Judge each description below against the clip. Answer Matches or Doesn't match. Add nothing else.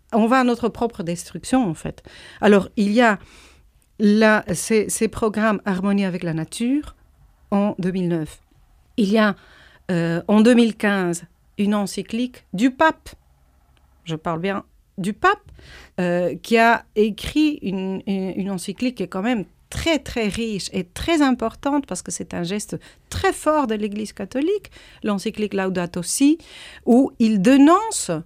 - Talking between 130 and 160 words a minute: Matches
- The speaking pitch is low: Doesn't match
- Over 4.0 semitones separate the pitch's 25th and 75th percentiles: Matches